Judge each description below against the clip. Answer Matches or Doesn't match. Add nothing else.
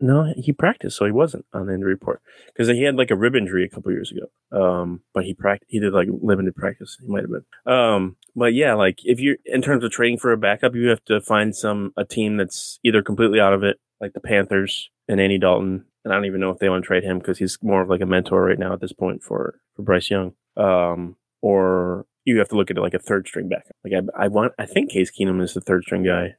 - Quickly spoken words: Matches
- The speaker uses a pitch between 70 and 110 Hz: Matches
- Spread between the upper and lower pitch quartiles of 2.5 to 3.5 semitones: Matches